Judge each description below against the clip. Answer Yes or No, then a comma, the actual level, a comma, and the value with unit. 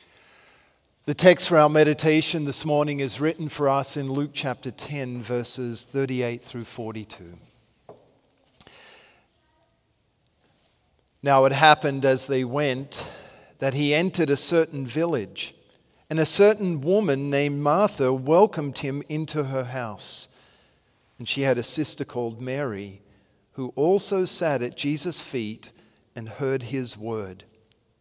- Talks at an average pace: No, slow, 125 wpm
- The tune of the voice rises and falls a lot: No, average, 3.8 semitones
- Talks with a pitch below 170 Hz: Yes, low, 135 Hz